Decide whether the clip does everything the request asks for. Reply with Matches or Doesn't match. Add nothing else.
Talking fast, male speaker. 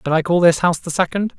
Matches